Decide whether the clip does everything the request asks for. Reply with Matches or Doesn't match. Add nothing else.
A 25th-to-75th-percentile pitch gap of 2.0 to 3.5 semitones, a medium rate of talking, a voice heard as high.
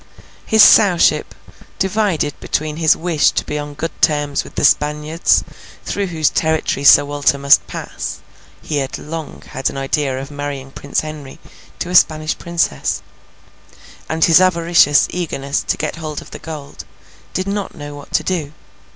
Doesn't match